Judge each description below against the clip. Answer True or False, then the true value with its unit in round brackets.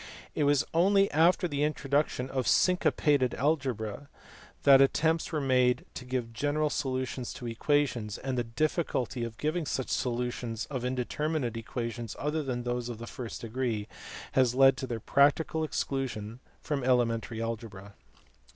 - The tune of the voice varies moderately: True (3.7 semitones)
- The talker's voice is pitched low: True (130 Hz)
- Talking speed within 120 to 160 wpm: True (150 wpm)